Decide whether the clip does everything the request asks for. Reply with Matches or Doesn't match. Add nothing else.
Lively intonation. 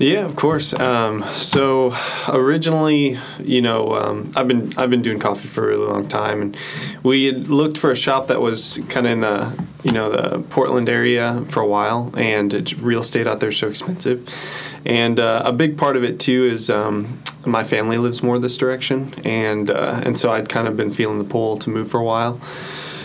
Doesn't match